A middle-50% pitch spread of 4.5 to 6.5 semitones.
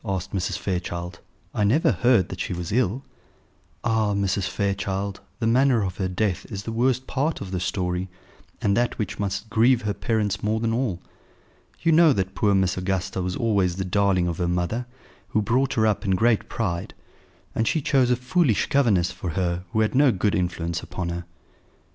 No: average, 4.1 semitones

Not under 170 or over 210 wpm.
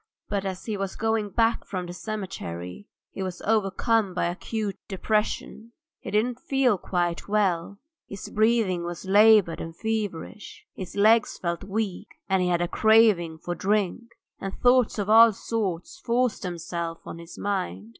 No: average, 155 wpm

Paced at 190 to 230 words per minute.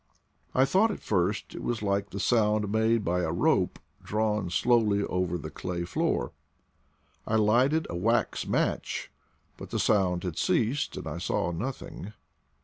No: average, 155 wpm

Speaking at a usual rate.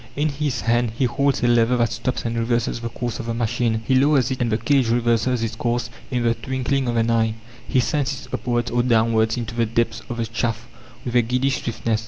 No: fast, 235 wpm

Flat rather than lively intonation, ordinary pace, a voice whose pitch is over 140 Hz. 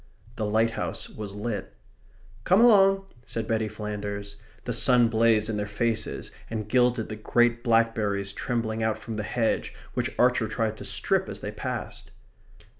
No: narrow, 2.0 semitones; average, 155 wpm; low, 110 Hz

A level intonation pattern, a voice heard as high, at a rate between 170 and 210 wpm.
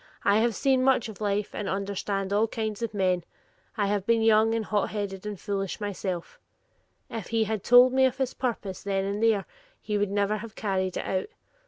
Yes: narrow, 2.3 semitones; high, 210 Hz; fast, 205 wpm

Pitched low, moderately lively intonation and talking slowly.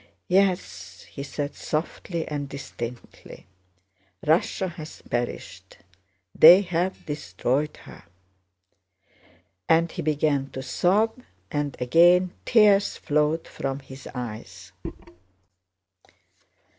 No: medium, 155 Hz; average, 4.5 semitones; slow, 85 wpm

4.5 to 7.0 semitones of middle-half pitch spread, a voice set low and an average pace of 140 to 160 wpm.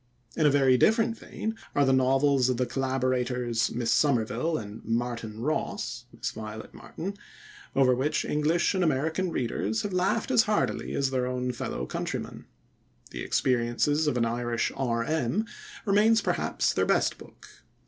Yes: average, 5.0 semitones; low, 130 Hz; average, 150 wpm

